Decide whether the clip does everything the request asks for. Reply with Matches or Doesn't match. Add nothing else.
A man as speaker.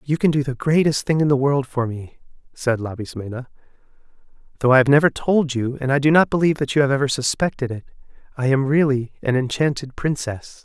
Matches